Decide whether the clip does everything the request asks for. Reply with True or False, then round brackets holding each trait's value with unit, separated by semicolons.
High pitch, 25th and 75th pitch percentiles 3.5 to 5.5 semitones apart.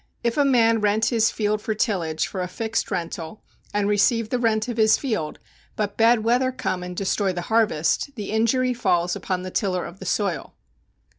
True (215 Hz; 3.8 semitones)